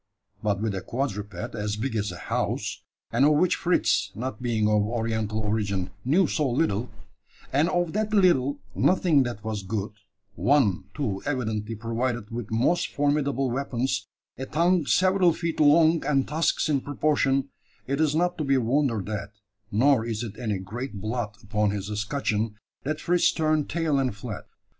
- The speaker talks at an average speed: Yes, average, 165 wpm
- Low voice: Yes, low, 125 Hz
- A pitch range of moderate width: No, wide, 5.7 semitones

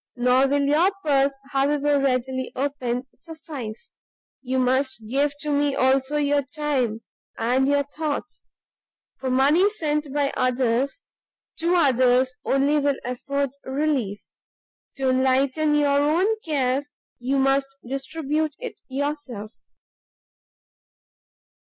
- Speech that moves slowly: Yes, slow, 110 wpm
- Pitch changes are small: Yes, narrow, 2.2 semitones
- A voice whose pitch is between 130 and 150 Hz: No, very high, 275 Hz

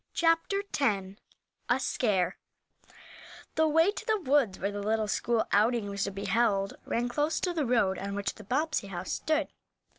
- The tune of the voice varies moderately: No, wide, 7.3 semitones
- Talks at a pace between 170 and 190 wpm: Yes, average, 175 wpm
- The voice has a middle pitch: No, high, 230 Hz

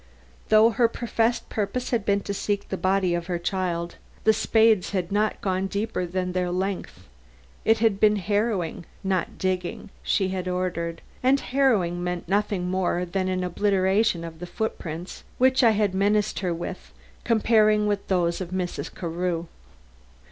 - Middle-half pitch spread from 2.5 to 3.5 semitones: Yes, average, 3.1 semitones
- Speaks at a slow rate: No, average, 160 wpm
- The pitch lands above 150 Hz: Yes, high, 190 Hz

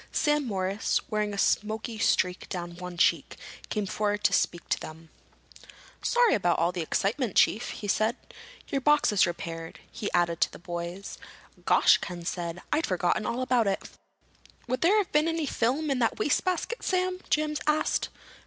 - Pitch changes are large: Yes, wide, 8.6 semitones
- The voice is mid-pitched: No, high, 210 Hz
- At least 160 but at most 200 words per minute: Yes, average, 170 wpm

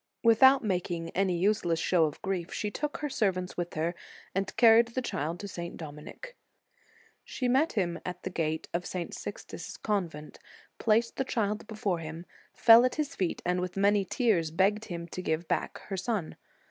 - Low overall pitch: No, high, 190 Hz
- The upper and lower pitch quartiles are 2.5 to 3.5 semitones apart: No, average, 4.6 semitones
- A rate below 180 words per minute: No, average, 185 wpm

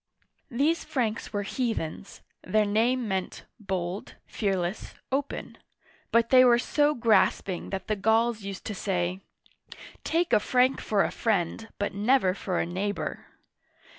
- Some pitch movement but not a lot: Yes, average, 4.0 semitones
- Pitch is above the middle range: Yes, high, 215 Hz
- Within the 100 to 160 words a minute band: Yes, average, 145 wpm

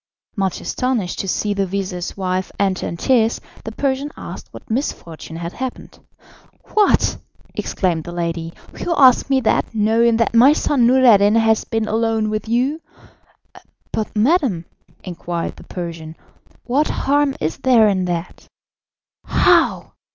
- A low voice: No, high, 220 Hz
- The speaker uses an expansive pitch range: Yes, wide, 5.7 semitones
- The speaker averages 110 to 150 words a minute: Yes, average, 140 wpm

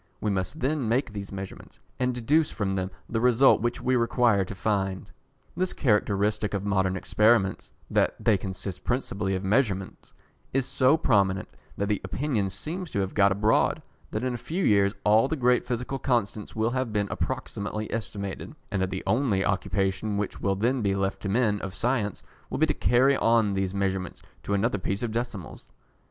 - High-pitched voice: No, low, 105 Hz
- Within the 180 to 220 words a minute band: Yes, average, 185 wpm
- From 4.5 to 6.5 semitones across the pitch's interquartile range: No, average, 4.0 semitones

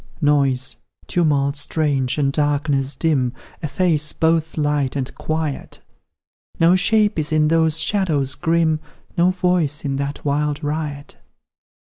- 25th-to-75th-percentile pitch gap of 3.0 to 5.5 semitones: No, narrow, 2.4 semitones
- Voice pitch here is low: No, medium, 150 Hz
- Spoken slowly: Yes, slow, 120 wpm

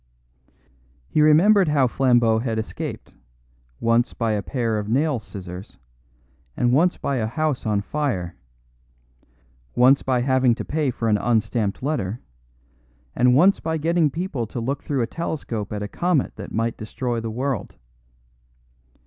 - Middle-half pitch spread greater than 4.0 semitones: Yes, average, 4.9 semitones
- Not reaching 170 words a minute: Yes, average, 150 wpm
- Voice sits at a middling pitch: No, low, 125 Hz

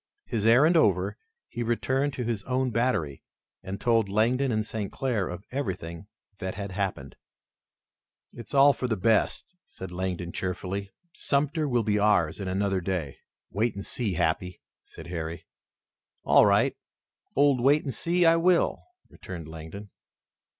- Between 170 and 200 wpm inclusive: No, average, 150 wpm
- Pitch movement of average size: No, wide, 5.7 semitones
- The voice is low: Yes, low, 105 Hz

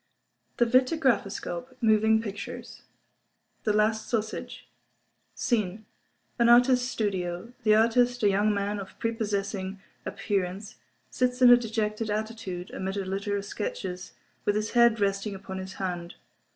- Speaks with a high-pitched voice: Yes, high, 215 Hz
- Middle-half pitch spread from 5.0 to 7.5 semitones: No, average, 2.9 semitones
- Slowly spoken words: Yes, slow, 125 wpm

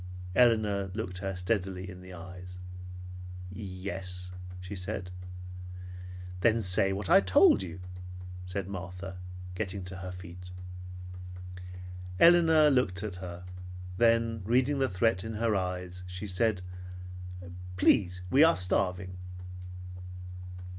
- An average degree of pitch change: Yes, average, 3.0 semitones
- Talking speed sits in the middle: No, slow, 115 wpm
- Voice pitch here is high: No, very low, 95 Hz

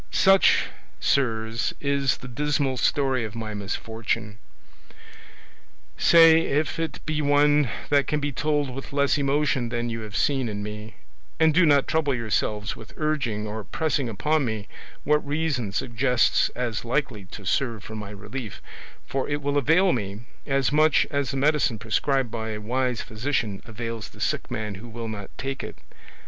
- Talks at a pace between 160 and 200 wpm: Yes, average, 165 wpm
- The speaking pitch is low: Yes, low, 125 Hz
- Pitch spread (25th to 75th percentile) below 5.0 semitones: Yes, average, 4.6 semitones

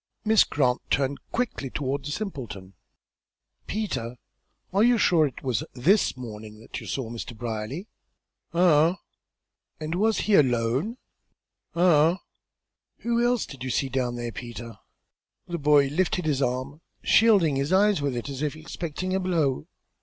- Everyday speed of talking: Yes, average, 155 wpm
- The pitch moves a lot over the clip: Yes, wide, 6.6 semitones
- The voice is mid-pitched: Yes, medium, 145 Hz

